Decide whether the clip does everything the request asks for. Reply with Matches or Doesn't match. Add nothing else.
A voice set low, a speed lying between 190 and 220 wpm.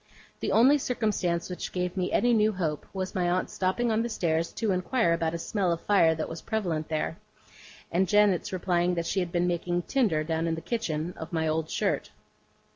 Doesn't match